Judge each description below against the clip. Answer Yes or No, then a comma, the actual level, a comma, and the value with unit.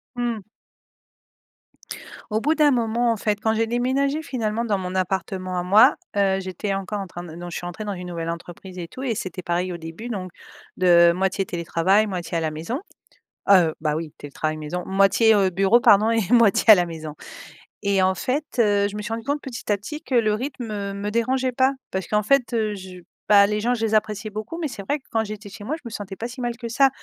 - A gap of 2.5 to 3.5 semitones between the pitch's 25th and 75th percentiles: No, average, 4.1 semitones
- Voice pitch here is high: Yes, high, 205 Hz